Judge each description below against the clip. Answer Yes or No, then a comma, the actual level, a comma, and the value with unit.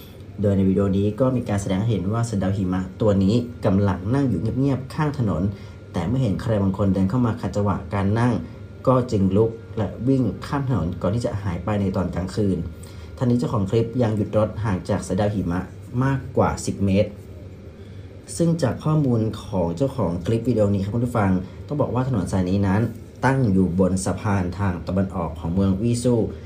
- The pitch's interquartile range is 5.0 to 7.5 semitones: No, average, 3.5 semitones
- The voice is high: No, low, 100 Hz